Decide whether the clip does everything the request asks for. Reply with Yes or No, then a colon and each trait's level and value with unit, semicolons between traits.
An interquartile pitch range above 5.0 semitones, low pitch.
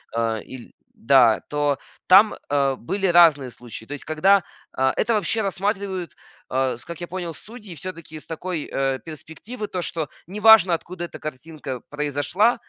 No: wide, 5.5 semitones; medium, 165 Hz